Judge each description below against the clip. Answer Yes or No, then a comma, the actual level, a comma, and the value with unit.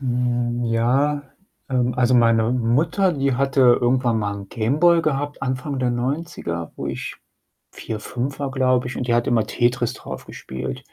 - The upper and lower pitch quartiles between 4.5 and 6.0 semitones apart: No, narrow, 2.5 semitones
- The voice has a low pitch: Yes, low, 125 Hz